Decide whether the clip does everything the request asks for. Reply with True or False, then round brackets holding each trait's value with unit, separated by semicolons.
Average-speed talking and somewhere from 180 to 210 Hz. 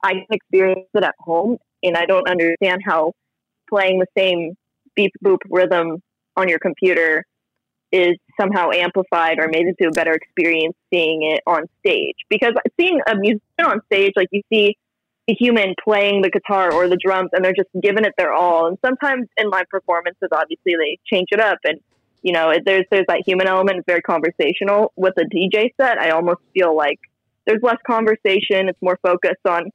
True (185 wpm; 190 Hz)